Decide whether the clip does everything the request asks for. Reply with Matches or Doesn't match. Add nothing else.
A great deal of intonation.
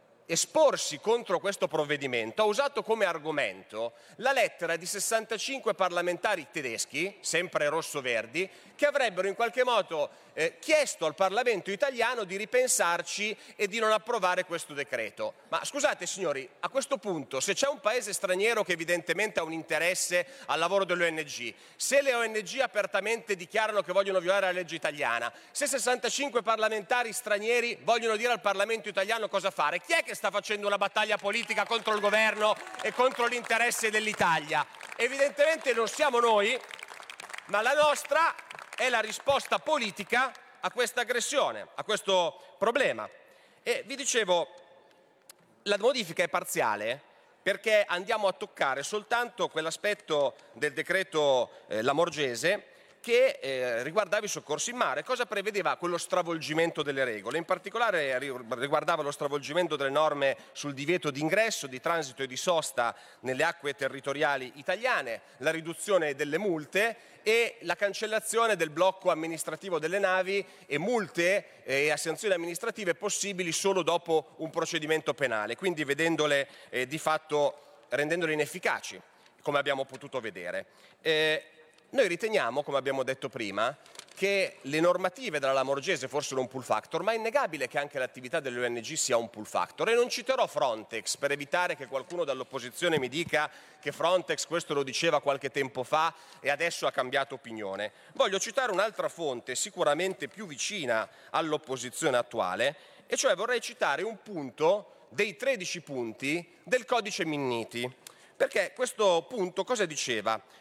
Matches